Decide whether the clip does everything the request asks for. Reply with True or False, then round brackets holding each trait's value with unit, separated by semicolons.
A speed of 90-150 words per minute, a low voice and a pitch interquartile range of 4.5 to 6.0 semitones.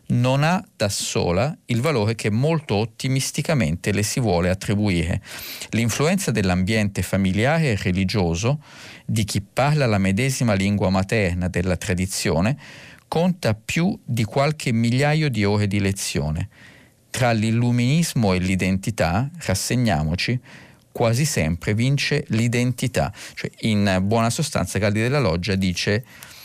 True (120 wpm; 110 Hz; 5.5 semitones)